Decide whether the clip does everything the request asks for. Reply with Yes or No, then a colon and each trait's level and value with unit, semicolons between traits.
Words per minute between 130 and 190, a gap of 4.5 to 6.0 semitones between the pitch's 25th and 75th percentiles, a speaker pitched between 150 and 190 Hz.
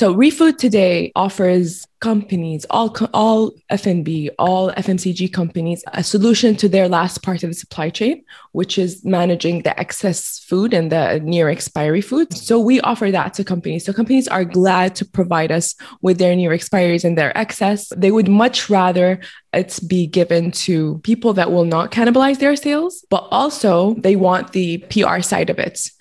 No: average, 175 wpm; average, 4.0 semitones; medium, 185 Hz